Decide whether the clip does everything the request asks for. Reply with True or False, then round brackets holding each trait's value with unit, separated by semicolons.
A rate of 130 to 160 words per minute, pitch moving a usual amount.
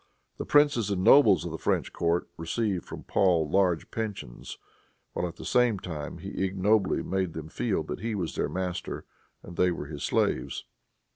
False (175 wpm; 3.9 semitones)